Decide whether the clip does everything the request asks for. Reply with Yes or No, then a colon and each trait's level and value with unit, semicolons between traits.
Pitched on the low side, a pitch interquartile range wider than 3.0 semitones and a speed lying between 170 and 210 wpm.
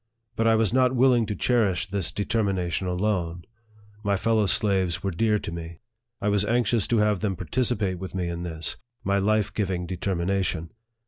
Yes: low, 100 Hz; average, 3.4 semitones; average, 180 wpm